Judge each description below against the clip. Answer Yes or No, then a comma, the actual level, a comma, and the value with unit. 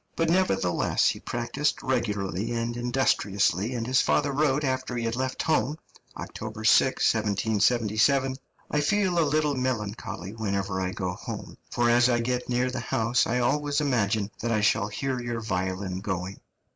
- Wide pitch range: No, average, 4.1 semitones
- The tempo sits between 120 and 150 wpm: No, average, 160 wpm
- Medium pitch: No, low, 120 Hz